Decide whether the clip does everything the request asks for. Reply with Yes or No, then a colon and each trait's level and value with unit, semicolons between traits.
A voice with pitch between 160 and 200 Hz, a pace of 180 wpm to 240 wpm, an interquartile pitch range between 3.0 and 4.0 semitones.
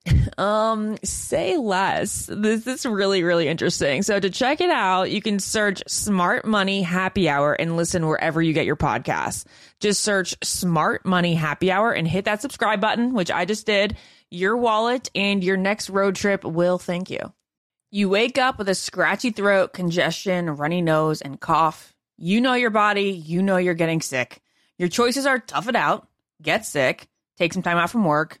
Yes: high, 190 Hz; average, 185 wpm; average, 3.5 semitones